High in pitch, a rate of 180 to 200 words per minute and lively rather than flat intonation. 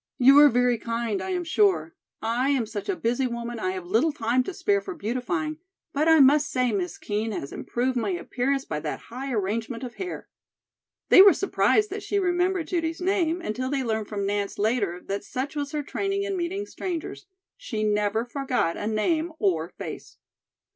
Yes: very high, 255 Hz; average, 190 wpm; wide, 7.2 semitones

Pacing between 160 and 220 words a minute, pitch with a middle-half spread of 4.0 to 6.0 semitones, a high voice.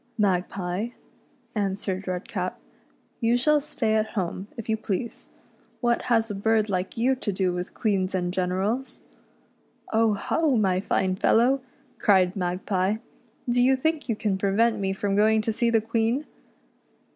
No: average, 170 wpm; average, 3.5 semitones; high, 210 Hz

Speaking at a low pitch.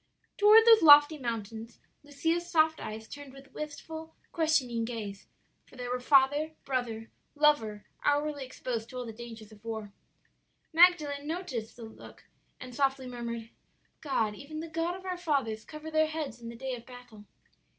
No: very high, 270 Hz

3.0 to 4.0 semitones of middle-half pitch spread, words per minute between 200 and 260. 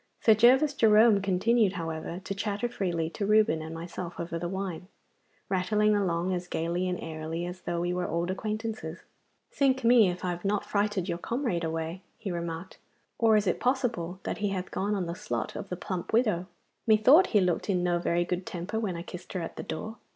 Yes: average, 3.6 semitones; fast, 205 wpm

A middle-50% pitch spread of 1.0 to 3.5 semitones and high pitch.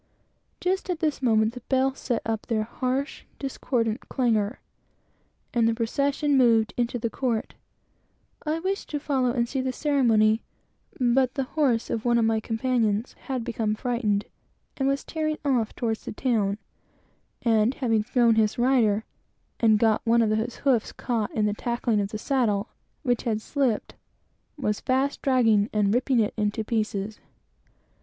Yes: average, 3.2 semitones; high, 235 Hz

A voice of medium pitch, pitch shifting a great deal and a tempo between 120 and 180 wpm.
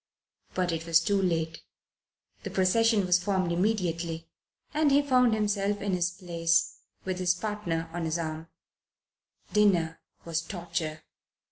No: medium, 180 Hz; average, 3.6 semitones; slow, 135 wpm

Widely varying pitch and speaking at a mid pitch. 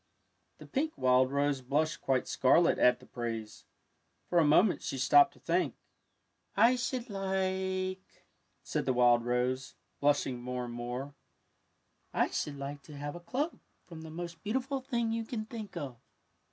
Yes: wide, 7.3 semitones; medium, 150 Hz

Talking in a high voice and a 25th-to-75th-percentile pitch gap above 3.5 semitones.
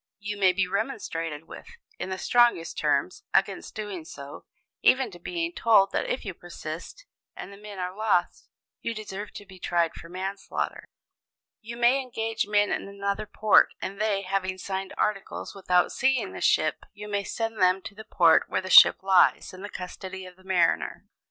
No: high, 195 Hz; average, 2.7 semitones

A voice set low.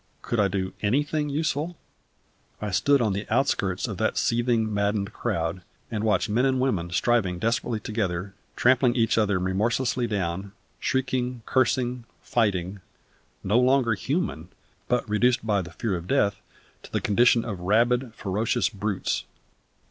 Yes: low, 110 Hz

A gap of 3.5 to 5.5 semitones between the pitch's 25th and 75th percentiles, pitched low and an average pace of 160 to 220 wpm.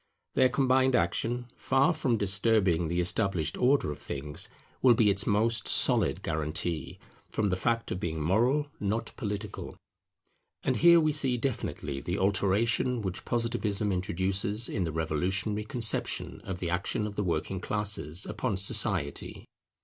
No: average, 4.8 semitones; low, 100 Hz; average, 145 wpm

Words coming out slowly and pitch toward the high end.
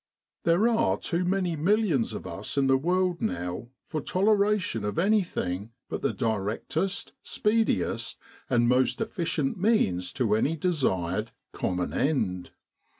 No: slow, 125 wpm; medium, 150 Hz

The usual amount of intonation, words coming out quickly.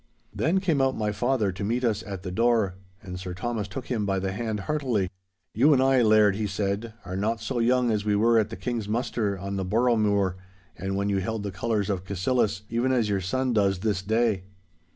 Yes: average, 3.4 semitones; fast, 220 wpm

